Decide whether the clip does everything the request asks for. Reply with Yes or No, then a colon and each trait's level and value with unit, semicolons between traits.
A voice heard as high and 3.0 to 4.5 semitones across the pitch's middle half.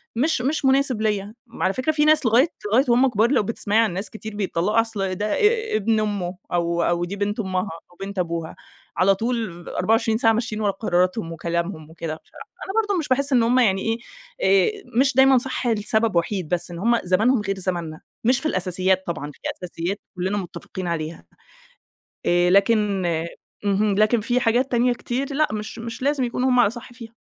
No: high, 215 Hz; average, 4.9 semitones